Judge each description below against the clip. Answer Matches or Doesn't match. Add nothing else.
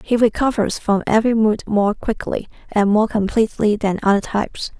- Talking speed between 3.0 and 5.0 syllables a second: Doesn't match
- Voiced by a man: Doesn't match